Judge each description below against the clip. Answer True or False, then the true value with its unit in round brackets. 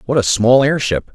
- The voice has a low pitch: True (125 Hz)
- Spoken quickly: True (210 wpm)